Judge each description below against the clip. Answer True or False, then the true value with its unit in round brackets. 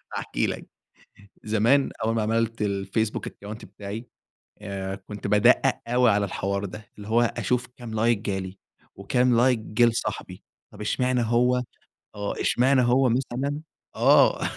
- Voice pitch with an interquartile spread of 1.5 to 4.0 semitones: True (3.3 semitones)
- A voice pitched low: True (115 Hz)